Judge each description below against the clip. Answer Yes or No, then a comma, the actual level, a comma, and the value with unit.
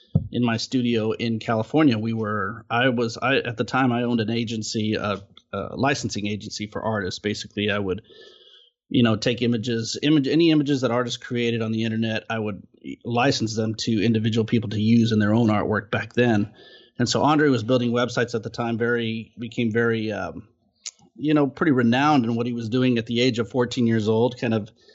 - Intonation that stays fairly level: Yes, narrow, 1.9 semitones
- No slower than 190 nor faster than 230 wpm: Yes, fast, 205 wpm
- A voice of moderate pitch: No, low, 115 Hz